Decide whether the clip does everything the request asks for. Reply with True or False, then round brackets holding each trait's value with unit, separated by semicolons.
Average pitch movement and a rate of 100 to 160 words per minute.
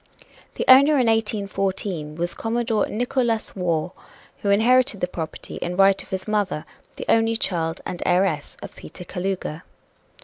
True (4.2 semitones; 145 wpm)